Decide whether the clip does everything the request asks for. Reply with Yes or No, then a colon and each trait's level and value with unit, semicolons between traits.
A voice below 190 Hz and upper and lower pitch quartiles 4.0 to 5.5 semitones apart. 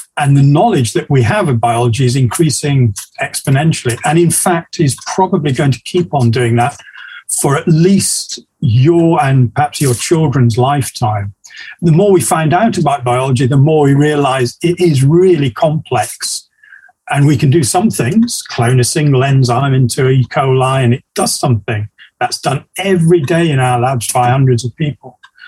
Yes: medium, 140 Hz; average, 5.1 semitones